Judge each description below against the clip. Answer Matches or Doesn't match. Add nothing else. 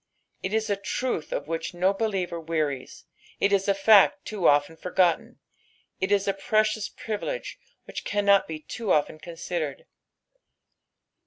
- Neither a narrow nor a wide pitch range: Matches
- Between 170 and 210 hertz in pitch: Matches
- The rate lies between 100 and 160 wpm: Matches